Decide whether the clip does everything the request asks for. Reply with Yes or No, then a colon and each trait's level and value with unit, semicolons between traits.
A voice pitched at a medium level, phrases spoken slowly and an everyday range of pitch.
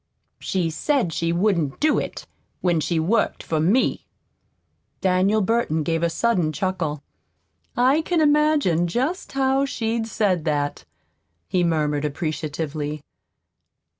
No: medium, 180 Hz; slow, 120 wpm; wide, 6.8 semitones